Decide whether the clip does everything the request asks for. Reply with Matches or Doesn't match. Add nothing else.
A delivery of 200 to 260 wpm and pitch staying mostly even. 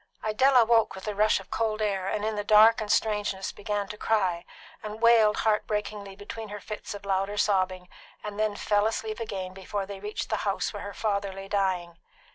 Matches